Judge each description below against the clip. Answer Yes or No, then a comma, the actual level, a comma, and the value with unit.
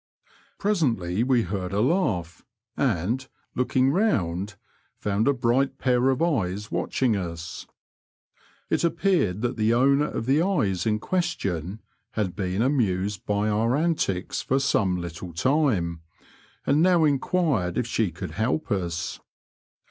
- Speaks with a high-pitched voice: No, low, 110 Hz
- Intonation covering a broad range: Yes, wide, 7.0 semitones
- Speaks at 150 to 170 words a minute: No, slow, 135 wpm